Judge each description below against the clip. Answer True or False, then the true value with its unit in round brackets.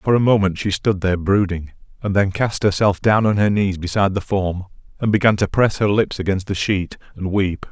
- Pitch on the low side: True (100 Hz)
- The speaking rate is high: True (225 wpm)